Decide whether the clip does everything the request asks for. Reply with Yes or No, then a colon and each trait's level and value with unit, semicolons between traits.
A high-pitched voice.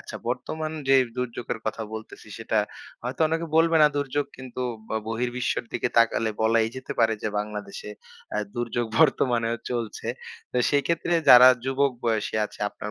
No: low, 120 Hz